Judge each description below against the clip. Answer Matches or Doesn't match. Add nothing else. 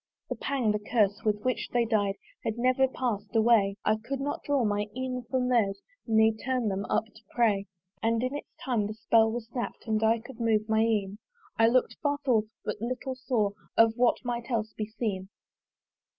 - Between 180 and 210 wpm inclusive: Matches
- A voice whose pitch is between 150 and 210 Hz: Doesn't match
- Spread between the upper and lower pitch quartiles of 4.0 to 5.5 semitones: Doesn't match